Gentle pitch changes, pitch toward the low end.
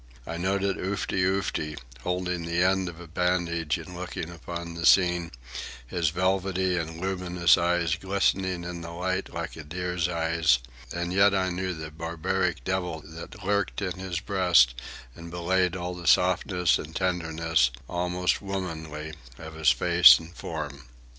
Yes: narrow, 1.9 semitones; very low, 90 Hz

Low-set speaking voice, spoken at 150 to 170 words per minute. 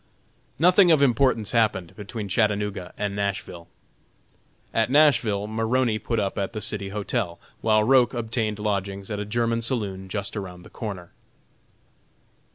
No: low, 105 Hz; average, 140 wpm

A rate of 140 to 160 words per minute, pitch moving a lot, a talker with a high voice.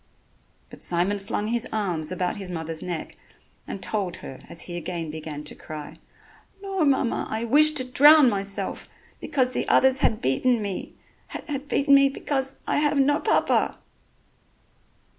Yes: average, 155 wpm; wide, 7.9 semitones; high, 220 Hz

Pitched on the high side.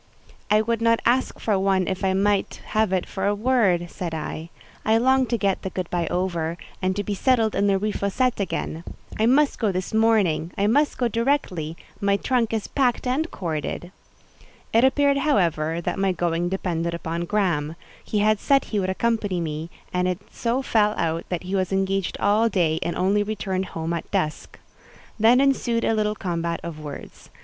Yes: high, 195 Hz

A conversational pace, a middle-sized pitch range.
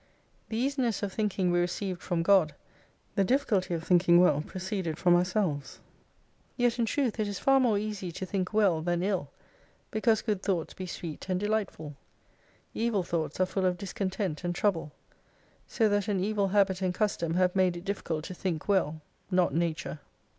Yes: average, 175 wpm; average, 3.1 semitones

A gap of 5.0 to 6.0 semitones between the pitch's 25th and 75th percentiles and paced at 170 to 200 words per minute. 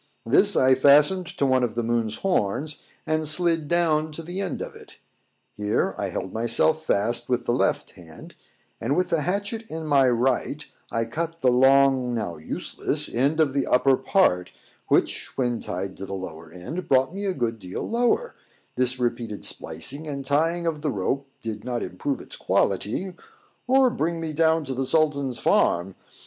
Yes: wide, 5.5 semitones; average, 180 wpm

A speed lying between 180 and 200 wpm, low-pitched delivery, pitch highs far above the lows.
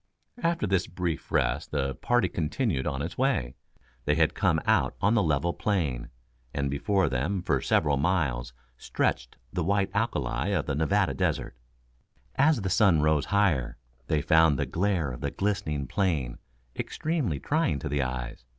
No: average, 160 wpm; very low, 80 Hz; wide, 6.1 semitones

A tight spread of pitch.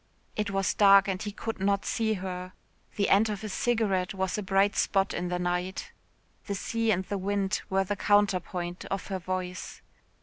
Yes: narrow, 1.7 semitones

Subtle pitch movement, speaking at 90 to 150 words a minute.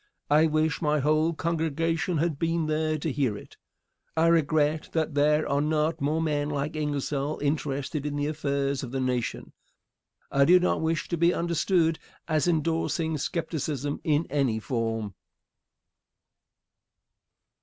Yes: narrow, 2.3 semitones; average, 140 wpm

